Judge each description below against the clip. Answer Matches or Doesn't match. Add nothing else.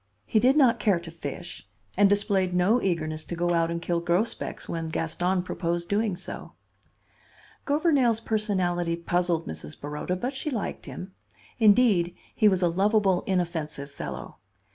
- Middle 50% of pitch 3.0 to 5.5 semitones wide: Matches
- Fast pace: Doesn't match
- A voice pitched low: Doesn't match